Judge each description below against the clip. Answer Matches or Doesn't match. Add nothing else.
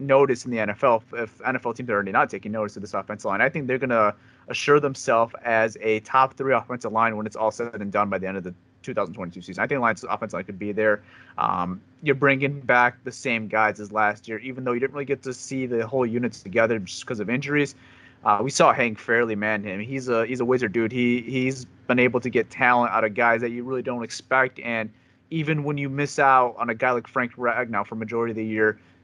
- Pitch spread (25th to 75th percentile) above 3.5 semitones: Doesn't match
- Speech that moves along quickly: Matches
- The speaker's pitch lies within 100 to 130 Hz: Matches